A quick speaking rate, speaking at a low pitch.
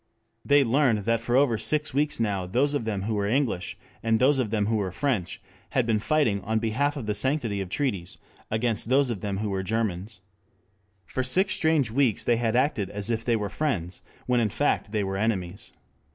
Yes: fast, 210 wpm; low, 115 Hz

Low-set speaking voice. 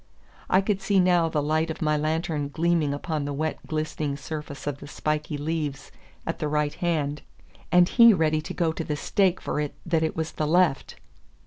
No: medium, 155 Hz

